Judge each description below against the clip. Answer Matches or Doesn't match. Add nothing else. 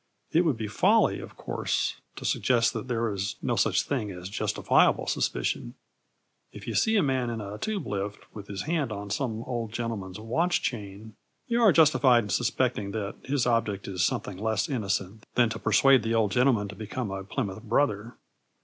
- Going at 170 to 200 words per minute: Matches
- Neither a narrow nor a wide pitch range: Matches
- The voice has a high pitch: Doesn't match